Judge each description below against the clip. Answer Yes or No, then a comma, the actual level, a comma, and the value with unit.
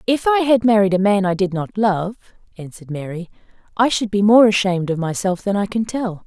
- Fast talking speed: Yes, fast, 220 wpm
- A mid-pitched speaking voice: No, high, 200 Hz